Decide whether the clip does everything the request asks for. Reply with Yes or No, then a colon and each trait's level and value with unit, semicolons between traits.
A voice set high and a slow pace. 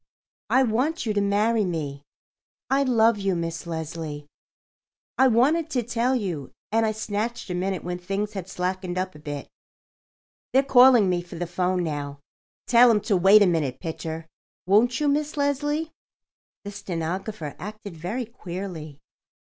No: high, 200 Hz; average, 155 wpm